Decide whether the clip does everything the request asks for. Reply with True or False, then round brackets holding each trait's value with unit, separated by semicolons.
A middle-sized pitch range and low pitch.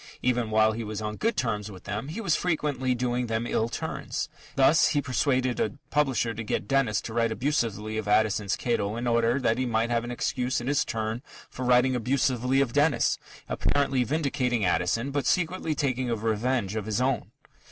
True (3.4 semitones; 120 Hz)